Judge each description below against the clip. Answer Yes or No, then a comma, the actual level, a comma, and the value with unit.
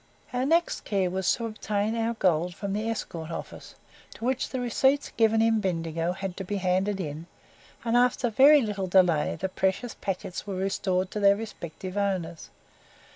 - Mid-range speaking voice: No, high, 200 Hz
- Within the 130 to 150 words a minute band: No, average, 180 wpm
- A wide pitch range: No, average, 3.8 semitones